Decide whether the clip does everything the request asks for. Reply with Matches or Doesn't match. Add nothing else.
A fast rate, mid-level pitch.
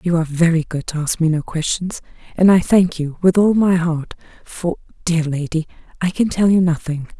Matches